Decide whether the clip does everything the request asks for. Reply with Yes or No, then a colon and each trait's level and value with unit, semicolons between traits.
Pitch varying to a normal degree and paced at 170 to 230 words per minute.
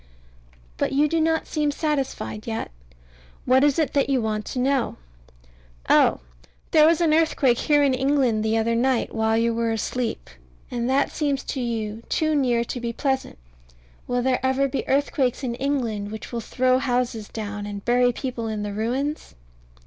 Yes: average, 3.6 semitones; average, 175 wpm